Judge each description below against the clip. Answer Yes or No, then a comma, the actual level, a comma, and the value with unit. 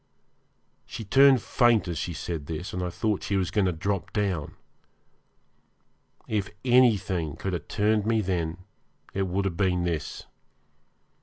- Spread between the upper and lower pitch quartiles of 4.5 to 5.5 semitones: No, average, 3.5 semitones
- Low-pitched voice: Yes, very low, 95 Hz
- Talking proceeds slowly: No, average, 150 wpm